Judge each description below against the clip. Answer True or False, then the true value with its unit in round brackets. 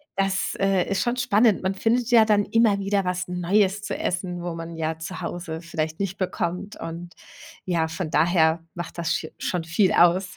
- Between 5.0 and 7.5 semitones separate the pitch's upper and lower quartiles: False (2.7 semitones)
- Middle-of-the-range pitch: True (180 Hz)